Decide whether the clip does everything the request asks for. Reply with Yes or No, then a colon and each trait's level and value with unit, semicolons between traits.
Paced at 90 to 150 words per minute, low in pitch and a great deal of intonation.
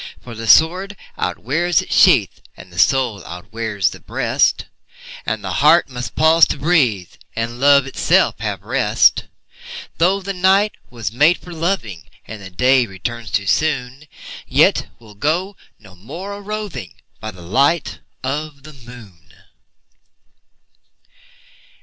Yes: slow, 135 wpm; low, 130 Hz; wide, 7.4 semitones